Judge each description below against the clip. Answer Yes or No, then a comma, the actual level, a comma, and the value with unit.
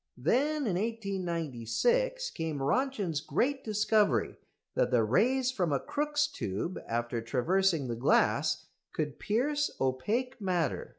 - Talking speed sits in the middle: No, slow, 120 wpm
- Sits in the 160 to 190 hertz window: Yes, medium, 185 Hz